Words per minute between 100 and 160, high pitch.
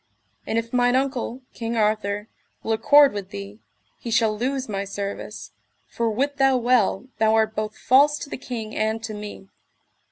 No: average, 170 wpm; high, 225 Hz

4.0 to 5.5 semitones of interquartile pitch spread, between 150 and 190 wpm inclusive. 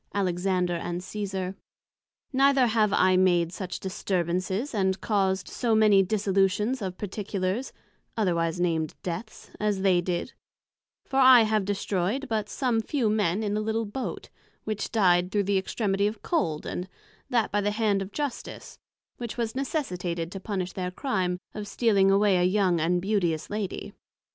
No: average, 3.1 semitones; average, 155 wpm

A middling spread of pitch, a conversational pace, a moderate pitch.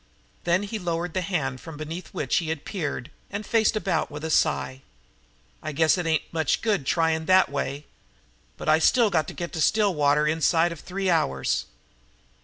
Yes: average, 3.4 semitones; average, 180 wpm; medium, 165 Hz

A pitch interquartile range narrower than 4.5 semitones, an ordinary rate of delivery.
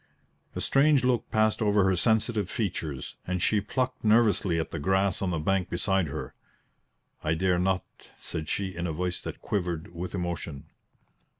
Yes: average, 3.5 semitones; average, 170 wpm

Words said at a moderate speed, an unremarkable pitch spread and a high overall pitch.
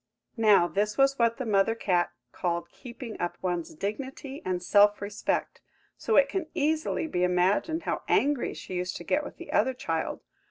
No: average, 175 wpm; wide, 7.1 semitones; high, 210 Hz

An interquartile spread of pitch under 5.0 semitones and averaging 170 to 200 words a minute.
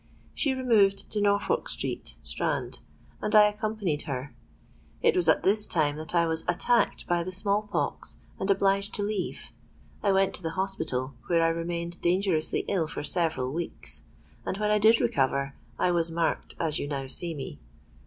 Yes: average, 4.0 semitones; average, 175 wpm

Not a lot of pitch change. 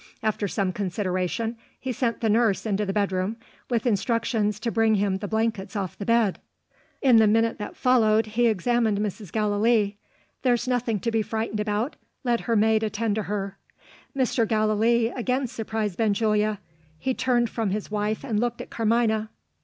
Yes: narrow, 2.0 semitones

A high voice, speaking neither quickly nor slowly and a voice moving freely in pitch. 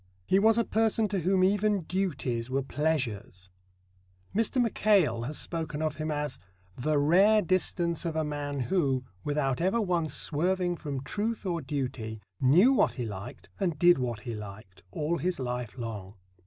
No: medium, 155 Hz; average, 165 wpm; wide, 6.5 semitones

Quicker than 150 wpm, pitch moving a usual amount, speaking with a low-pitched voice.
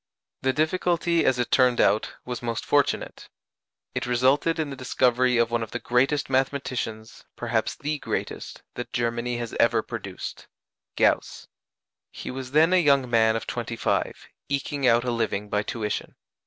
Yes: average, 160 wpm; average, 3.1 semitones; low, 125 Hz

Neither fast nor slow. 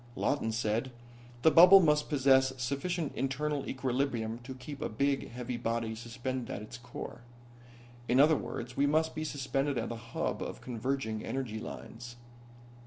Yes: average, 155 wpm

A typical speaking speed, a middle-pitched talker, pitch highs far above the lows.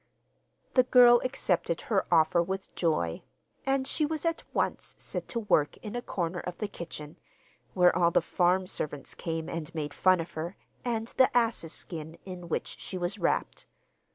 Yes: average, 175 wpm; medium, 180 Hz; wide, 5.7 semitones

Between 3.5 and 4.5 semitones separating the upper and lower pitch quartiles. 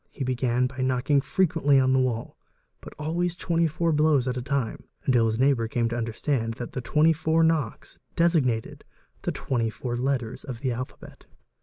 Yes: average, 4.2 semitones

